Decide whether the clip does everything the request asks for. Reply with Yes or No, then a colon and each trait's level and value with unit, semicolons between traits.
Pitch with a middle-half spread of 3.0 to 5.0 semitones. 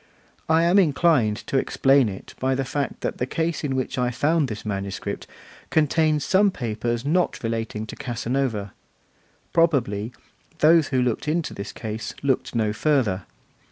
No: wide, 5.5 semitones